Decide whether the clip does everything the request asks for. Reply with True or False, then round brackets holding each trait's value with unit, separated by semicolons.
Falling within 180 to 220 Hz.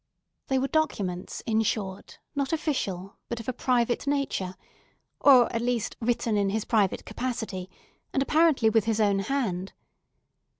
False (230 Hz)